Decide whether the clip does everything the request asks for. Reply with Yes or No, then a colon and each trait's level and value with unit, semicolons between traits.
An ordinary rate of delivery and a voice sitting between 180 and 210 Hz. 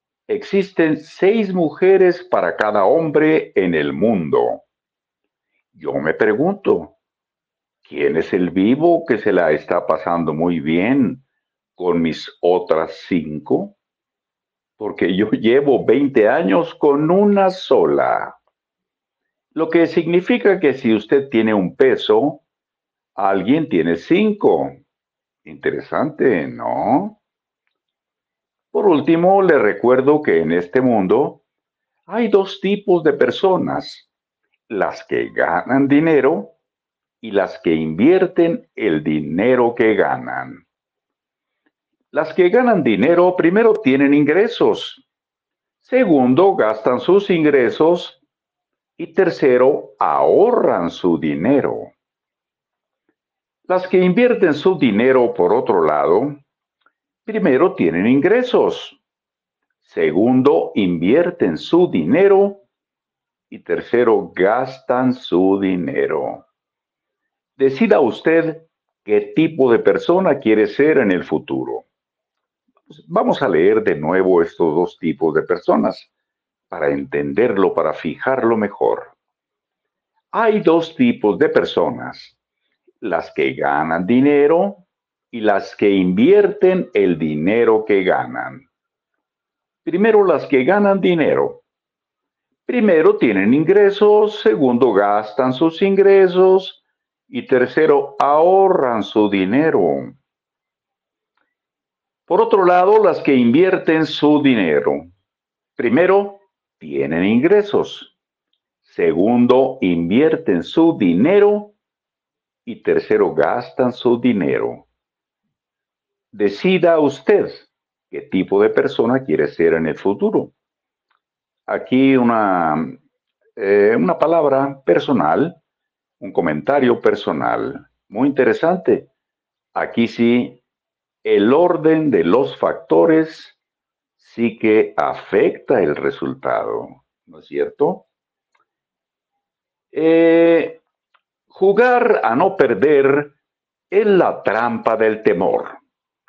No: slow, 95 wpm; medium, 185 Hz